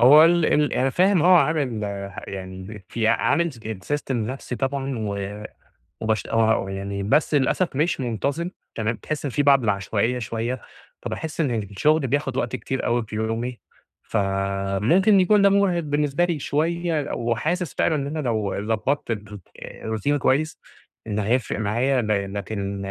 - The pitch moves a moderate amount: No, wide, 6.0 semitones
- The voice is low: Yes, low, 125 Hz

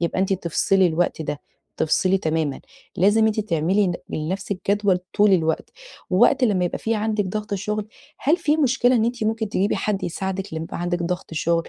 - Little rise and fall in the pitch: No, average, 3.7 semitones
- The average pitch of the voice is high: Yes, high, 195 Hz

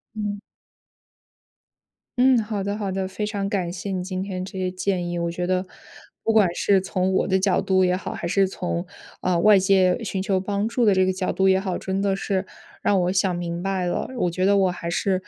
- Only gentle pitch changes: Yes, narrow, 1.5 semitones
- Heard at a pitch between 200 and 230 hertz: No, high, 190 Hz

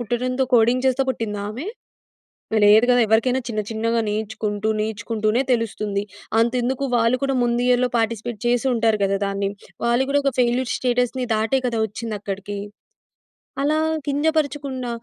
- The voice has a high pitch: Yes, high, 235 Hz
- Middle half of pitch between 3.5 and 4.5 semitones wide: No, average, 2.8 semitones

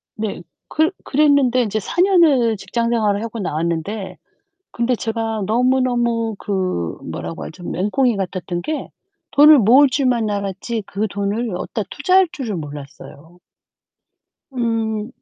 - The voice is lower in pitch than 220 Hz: No, high, 225 Hz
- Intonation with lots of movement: No, average, 4.4 semitones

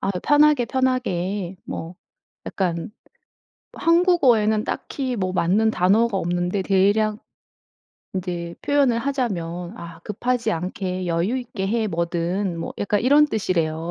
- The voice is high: Yes, high, 200 Hz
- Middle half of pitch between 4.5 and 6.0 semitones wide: Yes, wide, 5.4 semitones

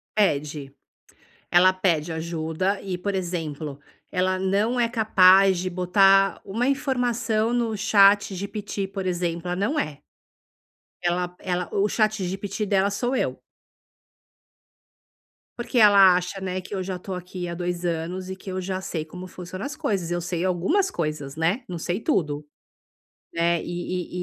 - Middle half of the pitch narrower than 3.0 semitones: Yes, narrow, 2.4 semitones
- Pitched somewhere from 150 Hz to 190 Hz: Yes, medium, 185 Hz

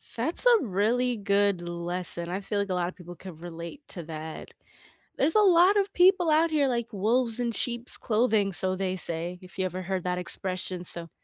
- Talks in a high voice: Yes, high, 195 Hz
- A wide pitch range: Yes, wide, 5.7 semitones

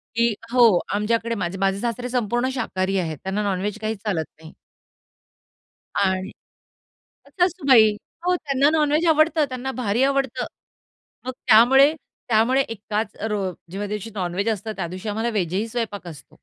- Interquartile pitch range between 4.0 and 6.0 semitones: Yes, average, 4.3 semitones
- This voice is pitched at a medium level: No, high, 225 Hz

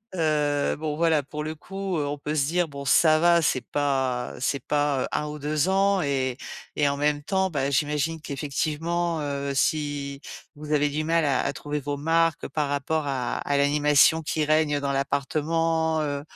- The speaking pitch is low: No, medium, 150 Hz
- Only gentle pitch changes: Yes, narrow, 2.0 semitones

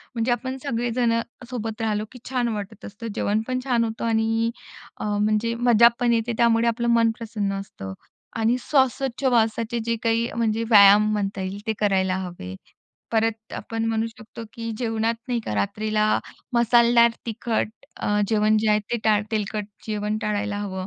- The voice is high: Yes, high, 225 Hz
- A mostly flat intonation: Yes, narrow, 1.9 semitones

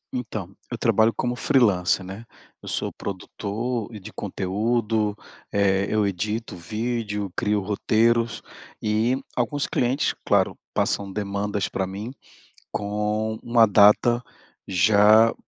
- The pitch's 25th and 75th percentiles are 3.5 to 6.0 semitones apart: No, narrow, 2.5 semitones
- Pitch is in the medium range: No, low, 105 Hz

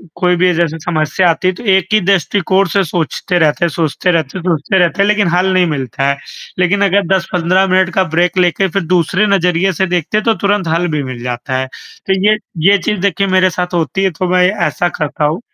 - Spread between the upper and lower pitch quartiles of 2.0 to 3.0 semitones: Yes, narrow, 2.6 semitones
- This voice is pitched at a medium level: Yes, medium, 180 Hz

